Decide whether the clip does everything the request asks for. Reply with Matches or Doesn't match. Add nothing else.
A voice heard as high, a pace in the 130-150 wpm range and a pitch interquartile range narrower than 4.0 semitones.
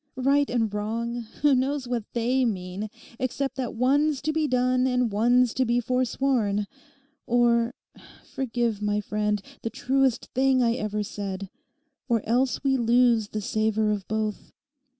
Matches